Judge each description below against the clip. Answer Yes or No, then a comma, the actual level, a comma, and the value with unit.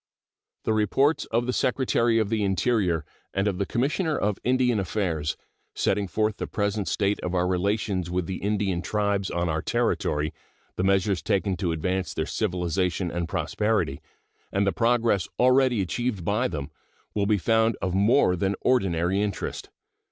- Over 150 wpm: Yes, average, 160 wpm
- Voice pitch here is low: Yes, low, 100 Hz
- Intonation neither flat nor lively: Yes, average, 3.7 semitones